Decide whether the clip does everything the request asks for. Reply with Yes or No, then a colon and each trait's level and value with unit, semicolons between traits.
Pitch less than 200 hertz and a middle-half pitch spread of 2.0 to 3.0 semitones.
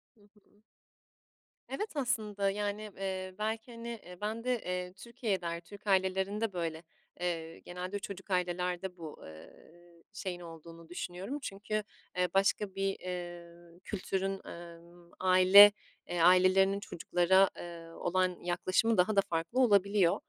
Yes: medium, 185 Hz; average, 2.7 semitones